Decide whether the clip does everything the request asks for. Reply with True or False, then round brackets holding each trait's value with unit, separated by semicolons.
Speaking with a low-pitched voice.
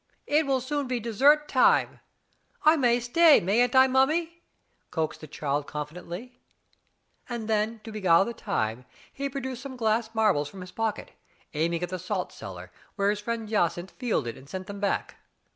False (220 Hz)